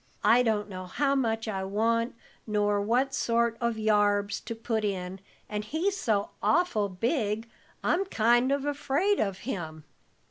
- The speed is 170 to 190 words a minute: No, average, 150 wpm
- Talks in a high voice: Yes, high, 225 Hz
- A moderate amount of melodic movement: Yes, average, 3.5 semitones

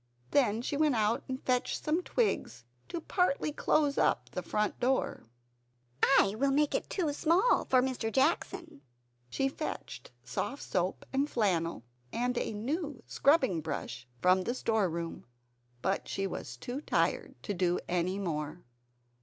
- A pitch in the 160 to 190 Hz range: No, high, 240 Hz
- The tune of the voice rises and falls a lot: Yes, wide, 7.5 semitones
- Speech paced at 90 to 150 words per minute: Yes, average, 145 wpm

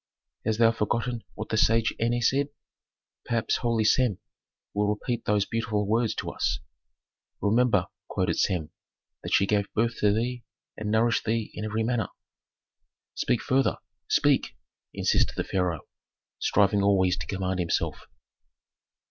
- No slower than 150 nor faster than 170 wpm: No, average, 140 wpm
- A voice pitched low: Yes, low, 110 Hz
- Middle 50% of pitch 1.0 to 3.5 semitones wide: Yes, narrow, 2.4 semitones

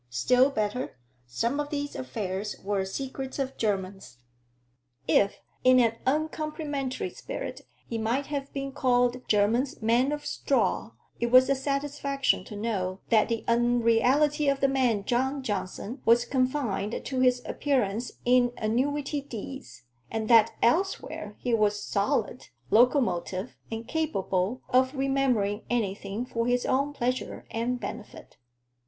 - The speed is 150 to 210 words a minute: No, slow, 135 wpm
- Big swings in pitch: No, average, 4.3 semitones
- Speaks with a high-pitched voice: Yes, high, 245 Hz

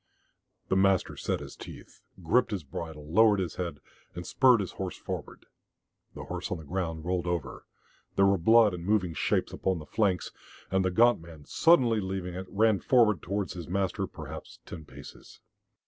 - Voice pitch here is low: Yes, very low, 95 Hz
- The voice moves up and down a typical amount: Yes, average, 3.5 semitones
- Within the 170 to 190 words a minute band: Yes, average, 180 wpm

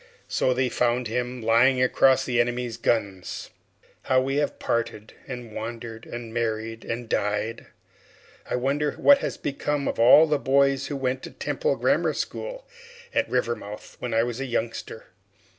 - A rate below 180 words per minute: Yes, average, 160 wpm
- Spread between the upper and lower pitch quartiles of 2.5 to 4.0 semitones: Yes, average, 2.8 semitones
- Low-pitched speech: Yes, low, 120 Hz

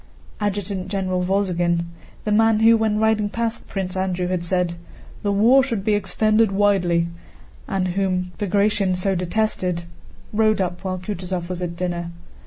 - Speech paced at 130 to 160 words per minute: Yes, average, 150 wpm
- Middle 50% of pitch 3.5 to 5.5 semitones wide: No, average, 2.8 semitones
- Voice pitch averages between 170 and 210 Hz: Yes, high, 190 Hz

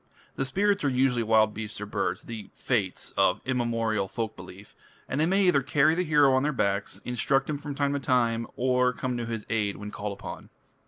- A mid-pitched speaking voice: No, low, 125 Hz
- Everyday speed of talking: No, fast, 210 wpm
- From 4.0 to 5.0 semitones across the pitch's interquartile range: Yes, average, 4.6 semitones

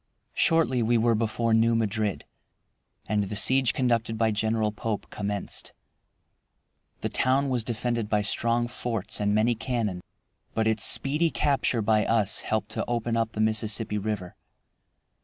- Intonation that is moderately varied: No, narrow, 2.0 semitones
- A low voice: Yes, low, 110 Hz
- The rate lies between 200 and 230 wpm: No, average, 145 wpm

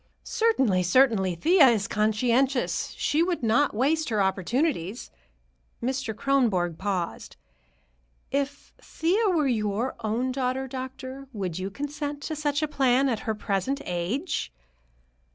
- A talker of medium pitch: No, very high, 255 Hz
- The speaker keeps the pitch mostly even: No, average, 5.2 semitones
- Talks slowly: Yes, slow, 125 wpm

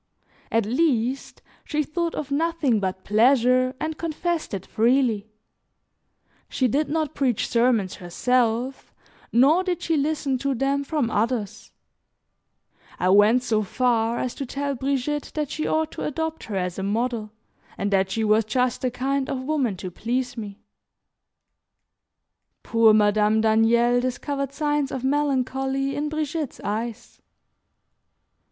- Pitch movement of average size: Yes, average, 4.2 semitones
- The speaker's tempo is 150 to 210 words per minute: No, slow, 135 wpm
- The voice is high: Yes, very high, 255 Hz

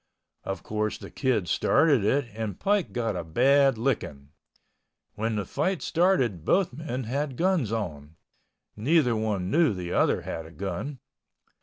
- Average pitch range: No, wide, 6.6 semitones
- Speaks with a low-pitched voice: Yes, low, 115 Hz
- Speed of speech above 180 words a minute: No, average, 150 wpm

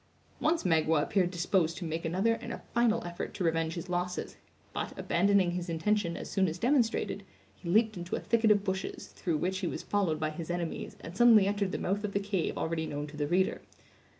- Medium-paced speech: No, fast, 215 wpm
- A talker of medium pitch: Yes, medium, 180 Hz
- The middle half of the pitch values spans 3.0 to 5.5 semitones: Yes, average, 3.5 semitones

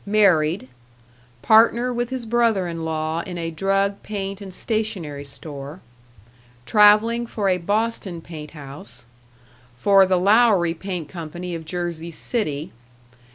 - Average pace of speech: No, slow, 125 wpm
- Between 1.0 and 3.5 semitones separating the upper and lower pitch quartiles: No, average, 4.8 semitones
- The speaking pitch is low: No, medium, 180 Hz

